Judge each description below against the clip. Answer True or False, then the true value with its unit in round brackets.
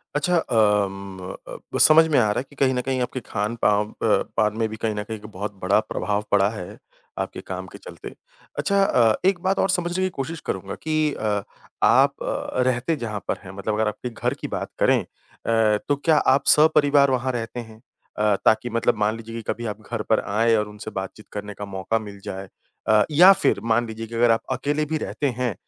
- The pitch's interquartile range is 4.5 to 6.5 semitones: True (4.9 semitones)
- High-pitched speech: False (115 Hz)